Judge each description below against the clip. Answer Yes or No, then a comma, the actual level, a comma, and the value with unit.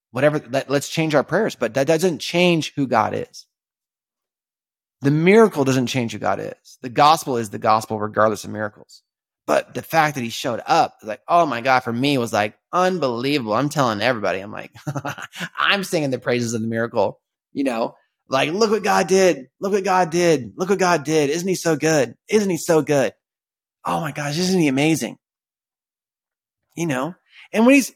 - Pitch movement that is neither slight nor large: No, wide, 5.7 semitones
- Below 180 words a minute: No, average, 195 wpm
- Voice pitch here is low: No, medium, 145 Hz